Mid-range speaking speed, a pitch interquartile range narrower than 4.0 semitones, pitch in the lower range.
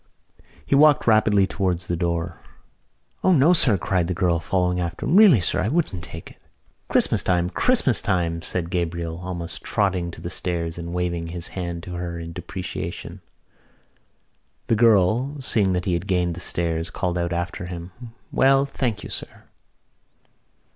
Yes: average, 160 wpm; average, 3.6 semitones; very low, 90 Hz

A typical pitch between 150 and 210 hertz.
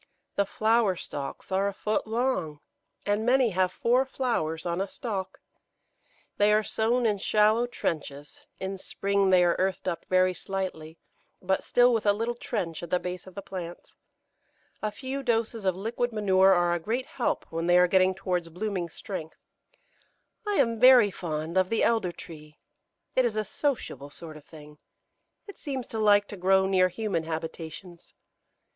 Yes: high, 190 Hz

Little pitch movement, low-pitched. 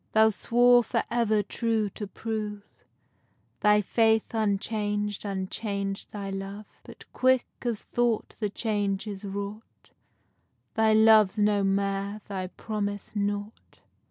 No: narrow, 1.7 semitones; high, 210 Hz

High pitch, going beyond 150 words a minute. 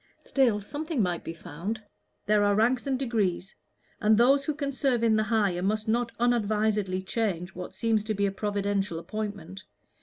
Yes: high, 215 Hz; average, 175 wpm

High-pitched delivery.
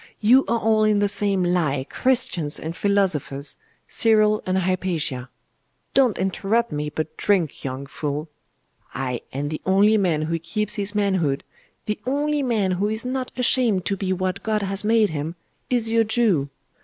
Yes: high, 195 Hz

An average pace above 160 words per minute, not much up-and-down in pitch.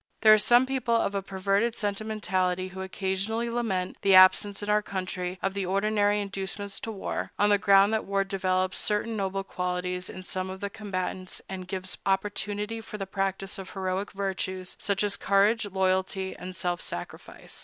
Yes: average, 175 wpm; narrow, 1.7 semitones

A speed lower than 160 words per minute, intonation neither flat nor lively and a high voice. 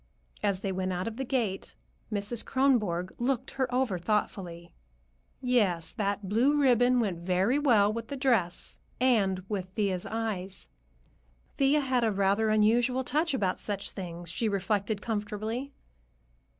Yes: average, 140 wpm; average, 4.5 semitones; high, 215 Hz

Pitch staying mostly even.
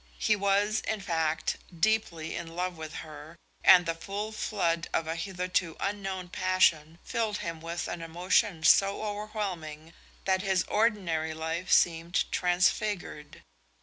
No: average, 3.5 semitones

